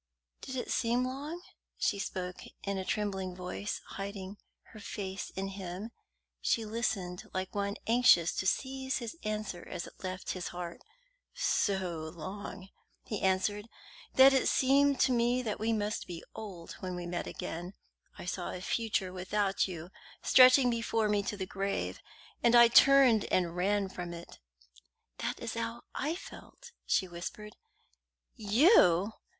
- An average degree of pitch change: Yes, average, 4.1 semitones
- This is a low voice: No, high, 200 Hz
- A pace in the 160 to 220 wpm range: No, average, 150 wpm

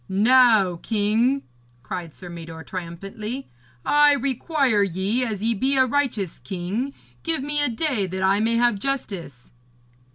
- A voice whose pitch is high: Yes, high, 220 Hz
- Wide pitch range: Yes, wide, 5.8 semitones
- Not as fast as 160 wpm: Yes, average, 140 wpm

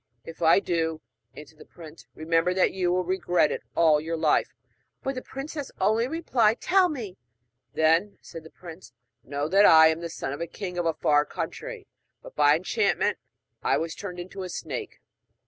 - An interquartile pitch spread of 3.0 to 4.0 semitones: No, average, 4.5 semitones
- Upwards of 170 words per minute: Yes, average, 185 wpm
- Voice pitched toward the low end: No, medium, 175 Hz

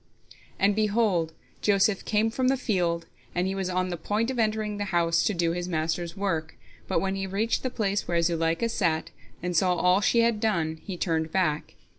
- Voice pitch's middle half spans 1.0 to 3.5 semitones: No, average, 3.9 semitones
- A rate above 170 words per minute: Yes, average, 200 wpm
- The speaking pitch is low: No, high, 190 Hz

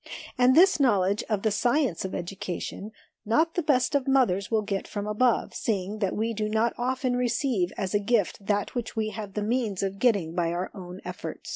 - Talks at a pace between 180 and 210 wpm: Yes, fast, 205 wpm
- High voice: Yes, high, 215 Hz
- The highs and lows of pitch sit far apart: No, average, 4.0 semitones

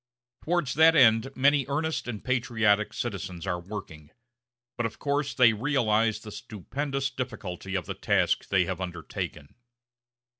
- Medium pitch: No, low, 115 Hz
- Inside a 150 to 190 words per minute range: No, average, 140 wpm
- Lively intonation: Yes, wide, 5.8 semitones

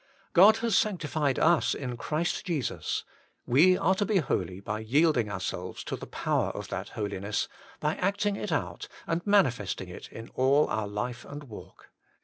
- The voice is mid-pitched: Yes, medium, 145 Hz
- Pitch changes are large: Yes, wide, 8.8 semitones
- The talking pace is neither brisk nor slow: Yes, average, 165 wpm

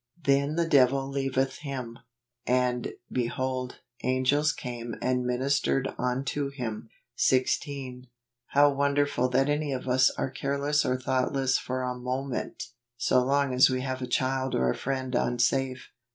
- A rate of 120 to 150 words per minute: Yes, average, 145 wpm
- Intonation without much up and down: Yes, narrow, 1.6 semitones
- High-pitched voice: No, low, 130 Hz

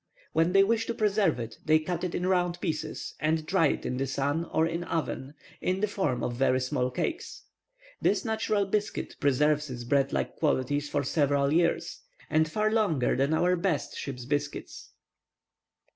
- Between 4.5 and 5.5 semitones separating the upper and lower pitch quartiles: Yes, average, 4.8 semitones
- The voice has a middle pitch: Yes, medium, 155 Hz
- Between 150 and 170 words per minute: No, average, 180 wpm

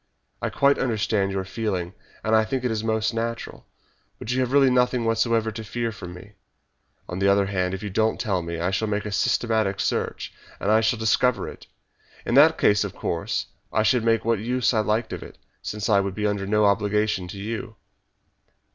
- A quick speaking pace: Yes, fast, 215 wpm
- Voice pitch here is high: No, low, 110 Hz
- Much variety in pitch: No, narrow, 2.6 semitones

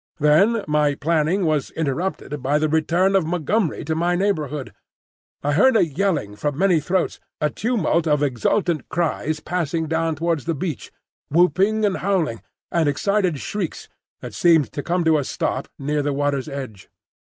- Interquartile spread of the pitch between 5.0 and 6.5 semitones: No, average, 3.6 semitones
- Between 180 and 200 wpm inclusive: No, average, 160 wpm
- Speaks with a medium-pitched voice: Yes, medium, 160 Hz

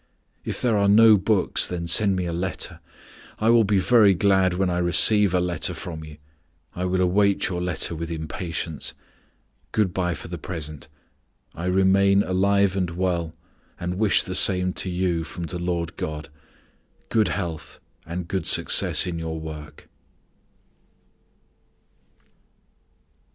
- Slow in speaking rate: No, average, 145 wpm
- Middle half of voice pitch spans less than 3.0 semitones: Yes, narrow, 2.5 semitones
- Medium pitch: No, very low, 90 Hz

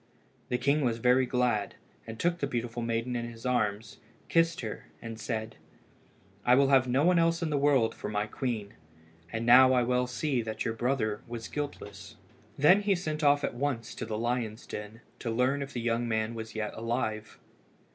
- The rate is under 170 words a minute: No, average, 195 wpm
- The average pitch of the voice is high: No, low, 120 Hz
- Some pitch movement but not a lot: Yes, average, 3.5 semitones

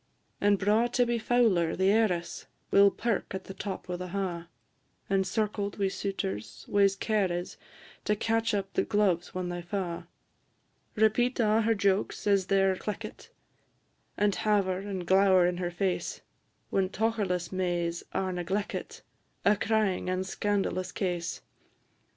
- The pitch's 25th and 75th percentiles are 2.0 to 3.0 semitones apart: Yes, narrow, 2.4 semitones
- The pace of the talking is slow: No, average, 145 wpm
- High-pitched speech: Yes, high, 195 Hz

